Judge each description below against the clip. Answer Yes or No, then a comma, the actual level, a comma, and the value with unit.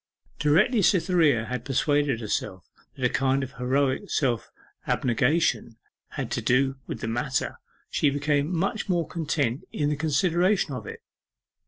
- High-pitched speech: No, medium, 140 Hz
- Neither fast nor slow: Yes, average, 145 wpm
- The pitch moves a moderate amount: Yes, average, 4.1 semitones